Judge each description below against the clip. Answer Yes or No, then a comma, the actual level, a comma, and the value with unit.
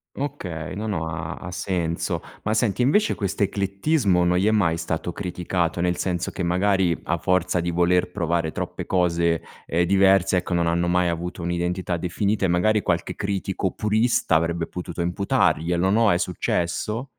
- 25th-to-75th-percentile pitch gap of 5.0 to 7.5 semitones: No, narrow, 2.4 semitones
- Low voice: Yes, very low, 90 Hz